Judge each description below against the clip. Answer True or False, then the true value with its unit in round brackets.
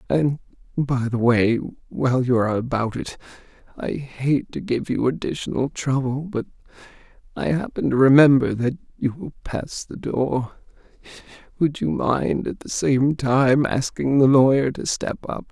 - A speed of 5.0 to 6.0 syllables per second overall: False (4.6 syllables/s)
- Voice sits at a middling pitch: False (125 Hz)